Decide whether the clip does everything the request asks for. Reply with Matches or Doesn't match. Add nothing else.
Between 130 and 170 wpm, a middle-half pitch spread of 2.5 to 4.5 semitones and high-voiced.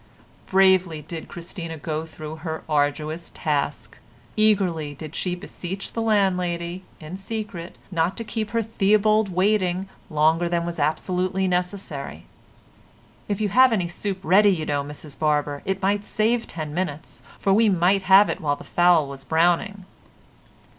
Doesn't match